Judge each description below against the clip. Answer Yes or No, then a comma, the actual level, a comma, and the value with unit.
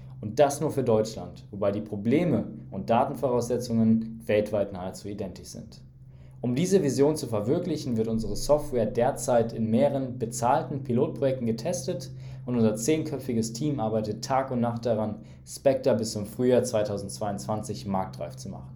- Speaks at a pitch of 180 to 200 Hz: No, low, 115 Hz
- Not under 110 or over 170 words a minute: Yes, average, 145 wpm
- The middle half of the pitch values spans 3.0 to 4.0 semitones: Yes, average, 3.6 semitones